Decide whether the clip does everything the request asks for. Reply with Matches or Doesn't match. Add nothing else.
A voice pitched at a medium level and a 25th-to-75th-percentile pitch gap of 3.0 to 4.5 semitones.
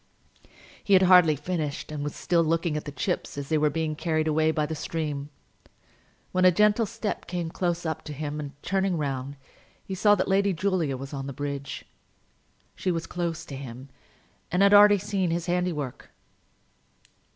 Matches